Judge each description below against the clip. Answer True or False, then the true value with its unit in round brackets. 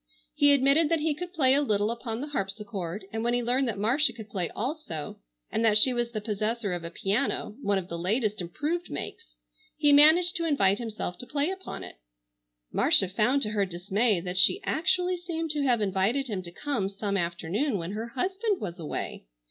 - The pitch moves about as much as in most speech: False (6.8 semitones)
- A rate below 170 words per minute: False (205 wpm)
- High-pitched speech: True (230 Hz)